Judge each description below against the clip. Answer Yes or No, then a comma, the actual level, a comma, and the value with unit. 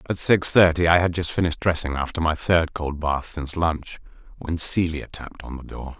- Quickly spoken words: Yes, fast, 210 wpm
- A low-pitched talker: Yes, very low, 80 Hz